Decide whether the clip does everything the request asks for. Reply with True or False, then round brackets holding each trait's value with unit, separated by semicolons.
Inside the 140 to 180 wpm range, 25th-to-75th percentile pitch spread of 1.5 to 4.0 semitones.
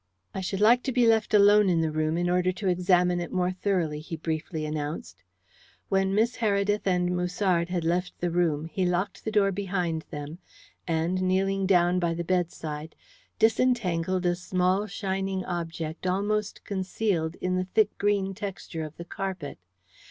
True (165 wpm; 2.8 semitones)